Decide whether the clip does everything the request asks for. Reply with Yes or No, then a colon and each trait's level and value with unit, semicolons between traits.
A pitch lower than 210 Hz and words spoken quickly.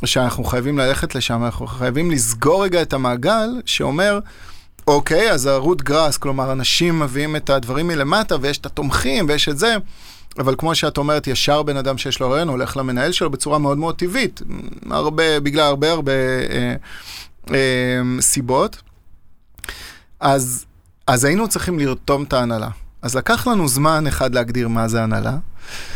Yes: low, 135 Hz; fast, 155 wpm